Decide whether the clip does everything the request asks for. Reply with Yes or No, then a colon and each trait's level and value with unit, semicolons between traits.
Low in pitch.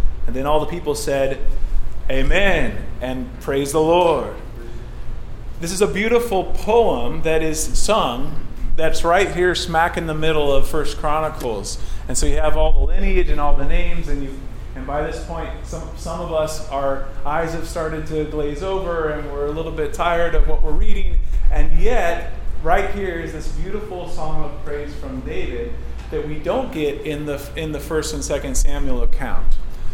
No: medium, 155 Hz